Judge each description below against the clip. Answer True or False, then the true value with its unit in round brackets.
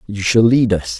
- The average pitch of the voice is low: True (115 Hz)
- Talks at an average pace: False (240 wpm)